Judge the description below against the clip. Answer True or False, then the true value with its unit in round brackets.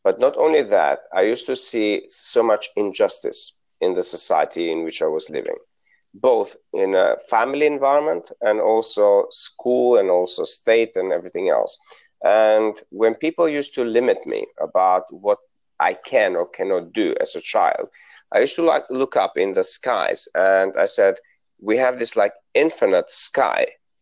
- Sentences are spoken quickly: False (170 wpm)